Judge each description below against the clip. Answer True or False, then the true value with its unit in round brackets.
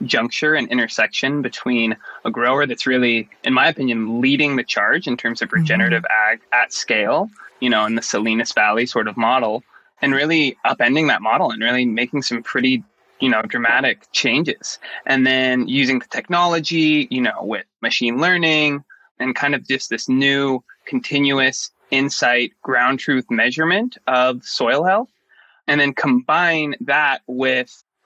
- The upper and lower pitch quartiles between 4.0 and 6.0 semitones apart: False (3.2 semitones)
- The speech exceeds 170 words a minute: False (155 wpm)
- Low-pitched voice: True (130 Hz)